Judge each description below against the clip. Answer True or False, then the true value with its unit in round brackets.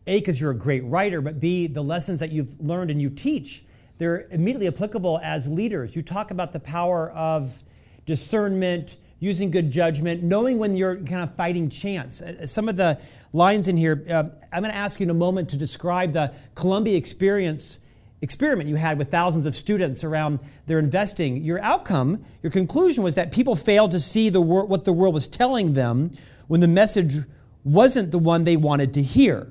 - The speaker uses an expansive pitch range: False (4.2 semitones)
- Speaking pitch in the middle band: True (170 Hz)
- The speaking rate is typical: True (195 wpm)